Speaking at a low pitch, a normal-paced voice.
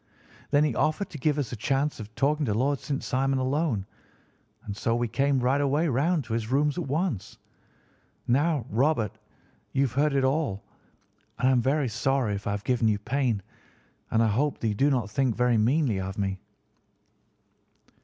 Yes: low, 130 Hz; average, 190 wpm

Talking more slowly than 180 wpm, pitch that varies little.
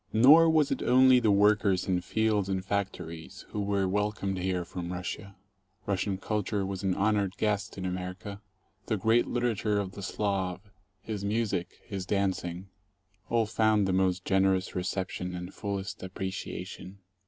Yes: average, 155 wpm; narrow, 2.2 semitones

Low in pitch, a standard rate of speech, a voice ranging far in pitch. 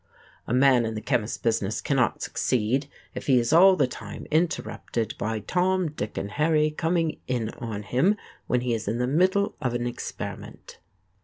Yes: low, 125 Hz; average, 175 wpm; wide, 5.7 semitones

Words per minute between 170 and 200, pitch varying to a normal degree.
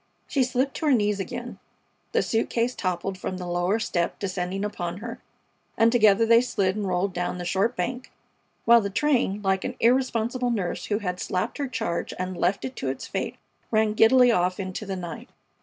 Yes: average, 195 wpm; average, 4.3 semitones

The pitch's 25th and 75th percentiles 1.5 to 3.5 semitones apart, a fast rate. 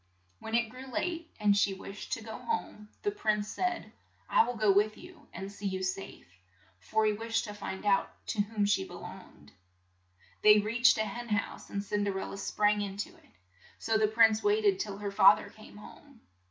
Yes: narrow, 2.4 semitones; fast, 210 wpm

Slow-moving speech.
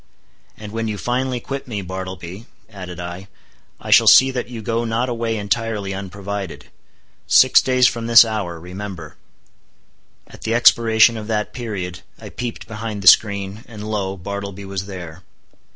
No: average, 155 wpm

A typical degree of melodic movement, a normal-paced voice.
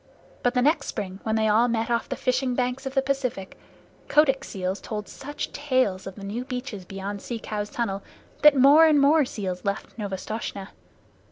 Yes: average, 5.0 semitones; average, 180 wpm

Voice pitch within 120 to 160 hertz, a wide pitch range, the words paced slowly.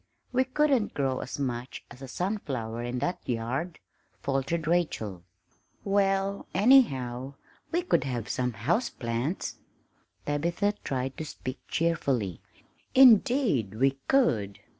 Yes: medium, 140 Hz; wide, 8.2 semitones; slow, 115 wpm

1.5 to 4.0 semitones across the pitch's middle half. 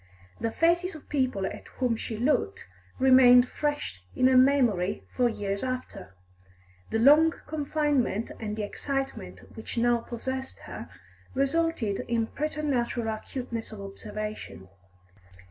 No: average, 4.4 semitones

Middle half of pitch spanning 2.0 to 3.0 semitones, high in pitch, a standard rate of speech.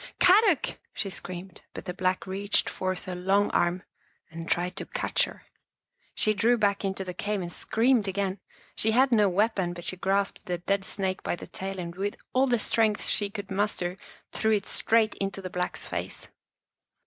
Yes: average, 2.7 semitones; high, 195 Hz; average, 190 wpm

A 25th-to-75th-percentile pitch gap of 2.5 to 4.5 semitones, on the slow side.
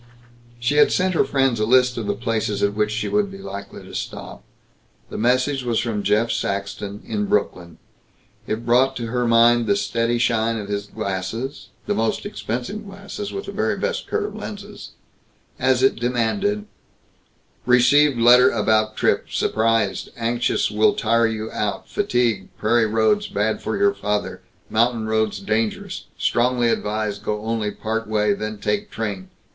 No: average, 3.0 semitones; average, 160 wpm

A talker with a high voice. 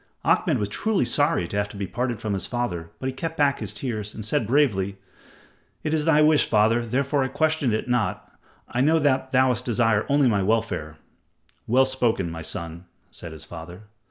No: low, 120 Hz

